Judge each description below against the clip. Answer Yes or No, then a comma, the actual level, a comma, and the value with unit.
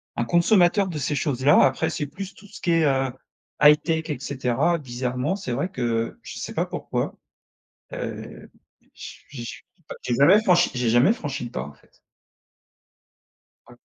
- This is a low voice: No, medium, 145 Hz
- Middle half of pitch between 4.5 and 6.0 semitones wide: Yes, wide, 5.5 semitones